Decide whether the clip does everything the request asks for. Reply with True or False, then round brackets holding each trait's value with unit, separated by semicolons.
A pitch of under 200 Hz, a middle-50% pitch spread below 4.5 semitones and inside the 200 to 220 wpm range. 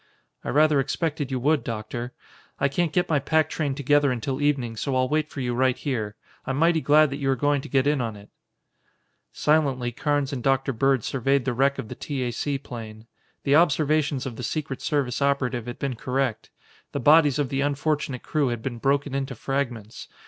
True (135 Hz; 2.8 semitones; 205 wpm)